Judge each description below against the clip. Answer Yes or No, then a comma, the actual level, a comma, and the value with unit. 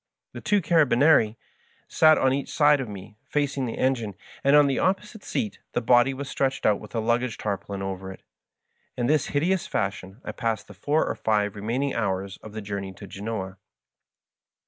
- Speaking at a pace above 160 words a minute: Yes, average, 190 wpm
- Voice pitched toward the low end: Yes, low, 120 Hz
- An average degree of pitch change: No, wide, 5.8 semitones